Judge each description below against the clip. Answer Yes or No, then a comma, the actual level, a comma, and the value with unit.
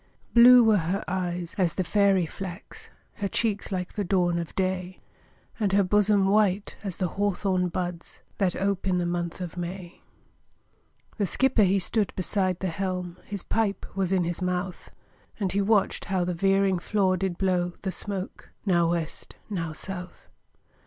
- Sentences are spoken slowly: No, average, 165 wpm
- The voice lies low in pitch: No, medium, 185 Hz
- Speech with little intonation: Yes, narrow, 1.9 semitones